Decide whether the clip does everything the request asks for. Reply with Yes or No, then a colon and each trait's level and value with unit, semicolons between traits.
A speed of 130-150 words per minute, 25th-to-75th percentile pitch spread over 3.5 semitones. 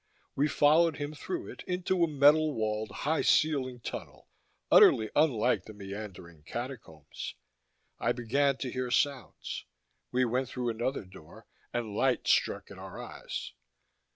Yes: average, 140 wpm; average, 5.1 semitones